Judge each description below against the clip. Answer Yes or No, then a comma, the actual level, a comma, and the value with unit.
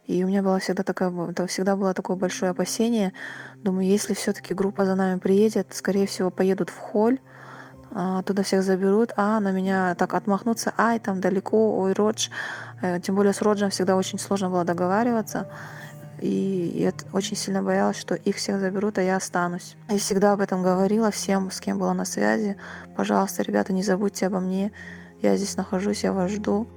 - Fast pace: Yes, fast, 180 wpm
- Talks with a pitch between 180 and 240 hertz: Yes, high, 190 Hz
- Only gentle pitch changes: Yes, narrow, 1.7 semitones